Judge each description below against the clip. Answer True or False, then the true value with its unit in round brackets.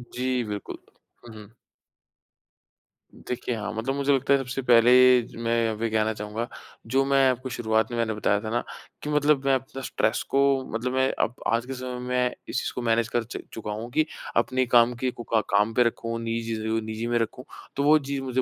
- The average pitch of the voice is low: True (120 Hz)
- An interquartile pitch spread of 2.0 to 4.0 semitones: True (2.4 semitones)